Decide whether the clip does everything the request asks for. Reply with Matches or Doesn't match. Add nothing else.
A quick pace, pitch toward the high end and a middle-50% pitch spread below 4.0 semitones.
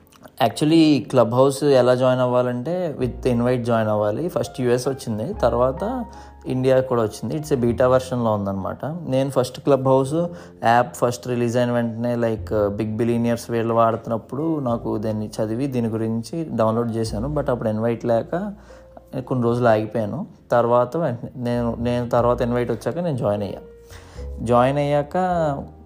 Doesn't match